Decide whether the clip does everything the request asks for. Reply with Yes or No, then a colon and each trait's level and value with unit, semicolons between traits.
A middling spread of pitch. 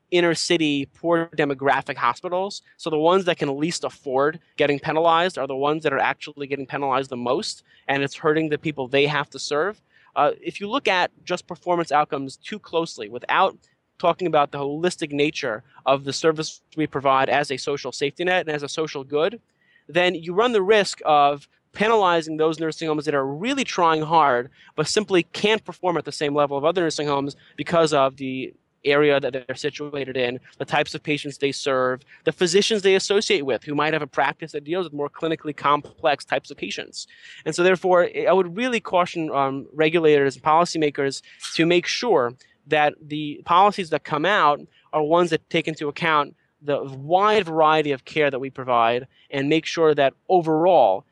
Yes: average, 3.4 semitones